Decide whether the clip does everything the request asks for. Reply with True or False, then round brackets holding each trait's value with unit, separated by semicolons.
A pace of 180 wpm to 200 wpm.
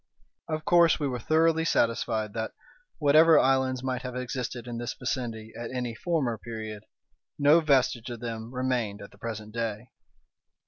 False (155 wpm)